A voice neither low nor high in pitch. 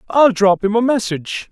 No: high, 215 Hz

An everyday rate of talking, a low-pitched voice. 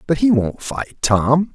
No: average, 195 wpm; medium, 145 Hz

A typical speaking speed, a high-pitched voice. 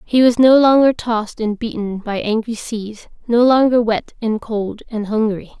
Yes: average, 180 wpm; high, 225 Hz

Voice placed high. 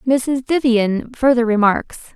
Yes: high, 245 Hz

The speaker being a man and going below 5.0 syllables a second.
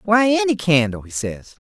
Yes: male; 4.7 syllables/s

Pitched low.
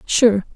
No: high, 215 Hz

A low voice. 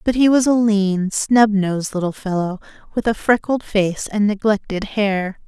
No: high, 205 Hz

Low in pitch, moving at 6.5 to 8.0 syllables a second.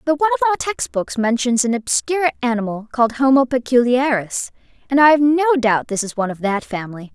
No: very high, 255 Hz; 7.4 syllables/s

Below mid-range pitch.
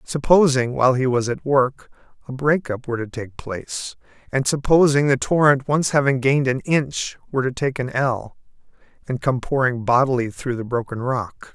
Yes: low, 130 Hz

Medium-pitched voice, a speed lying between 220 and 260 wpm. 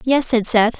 No: high, 235 Hz; fast, 225 wpm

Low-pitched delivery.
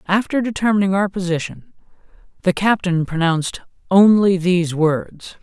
No: medium, 185 Hz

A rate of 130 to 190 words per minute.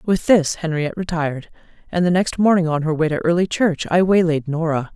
No: fast, 205 wpm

